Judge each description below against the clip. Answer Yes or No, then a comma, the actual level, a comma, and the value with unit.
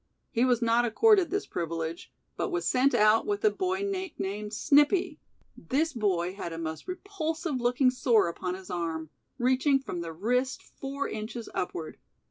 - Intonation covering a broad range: Yes, wide, 8.8 semitones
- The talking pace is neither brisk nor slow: Yes, average, 160 wpm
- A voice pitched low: No, high, 245 Hz